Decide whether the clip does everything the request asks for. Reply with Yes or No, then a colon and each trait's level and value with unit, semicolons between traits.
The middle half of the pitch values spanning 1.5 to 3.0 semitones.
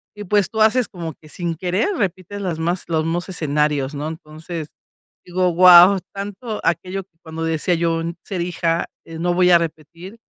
Yes: narrow, 2.5 semitones